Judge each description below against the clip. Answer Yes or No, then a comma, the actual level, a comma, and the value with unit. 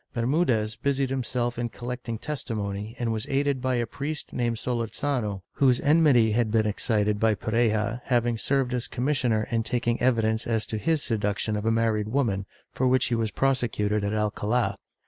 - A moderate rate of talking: Yes, average, 170 wpm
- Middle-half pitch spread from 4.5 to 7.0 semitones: No, average, 2.9 semitones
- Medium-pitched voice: No, low, 115 Hz